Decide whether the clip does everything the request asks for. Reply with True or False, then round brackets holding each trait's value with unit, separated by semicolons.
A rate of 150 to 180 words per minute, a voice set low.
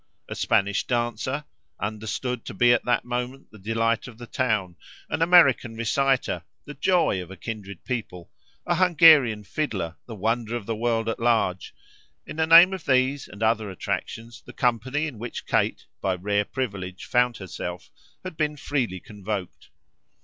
True (165 wpm; 115 Hz)